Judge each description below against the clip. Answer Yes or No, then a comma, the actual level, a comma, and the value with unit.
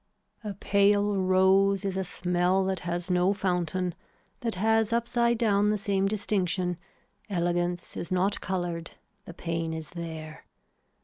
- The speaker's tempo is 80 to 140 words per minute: Yes, slow, 135 wpm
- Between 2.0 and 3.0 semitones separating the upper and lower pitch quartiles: Yes, narrow, 2.4 semitones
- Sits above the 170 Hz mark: Yes, medium, 185 Hz